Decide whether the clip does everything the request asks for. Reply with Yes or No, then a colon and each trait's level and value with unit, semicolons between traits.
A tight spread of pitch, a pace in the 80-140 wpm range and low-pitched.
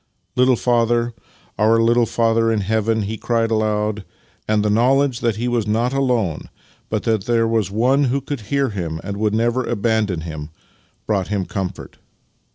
No: narrow, 2.2 semitones; average, 170 wpm; low, 115 Hz